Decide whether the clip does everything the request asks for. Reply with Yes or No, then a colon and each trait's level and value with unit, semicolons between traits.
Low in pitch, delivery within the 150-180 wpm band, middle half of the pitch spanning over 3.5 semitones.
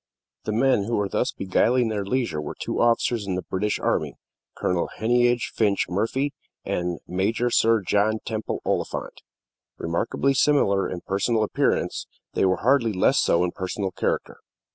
Yes: low, 105 Hz; average, 155 wpm; average, 4.0 semitones